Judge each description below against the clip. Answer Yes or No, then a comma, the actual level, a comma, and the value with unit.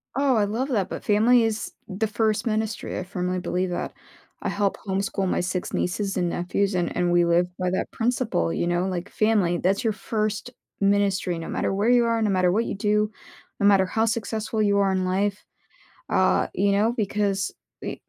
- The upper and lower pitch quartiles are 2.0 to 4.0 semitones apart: Yes, average, 2.9 semitones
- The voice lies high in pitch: Yes, high, 200 Hz